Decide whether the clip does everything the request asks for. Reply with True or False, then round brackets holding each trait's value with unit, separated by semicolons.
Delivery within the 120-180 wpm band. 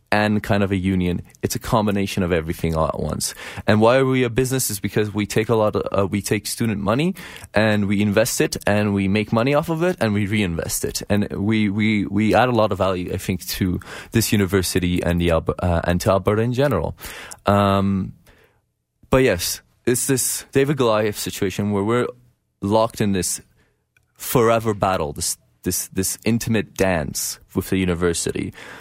False (190 wpm)